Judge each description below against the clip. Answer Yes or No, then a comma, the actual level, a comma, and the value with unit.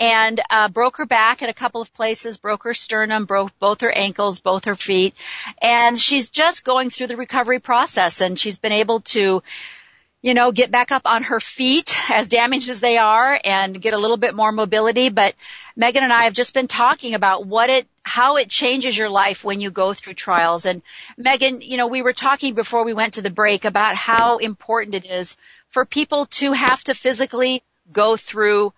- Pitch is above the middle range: Yes, high, 230 Hz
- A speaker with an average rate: No, fast, 210 wpm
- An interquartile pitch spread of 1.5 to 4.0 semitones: Yes, average, 3.5 semitones